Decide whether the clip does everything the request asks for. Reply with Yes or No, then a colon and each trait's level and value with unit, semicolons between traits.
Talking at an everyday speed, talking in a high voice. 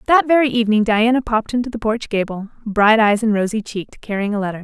No: fast, 220 wpm; high, 220 Hz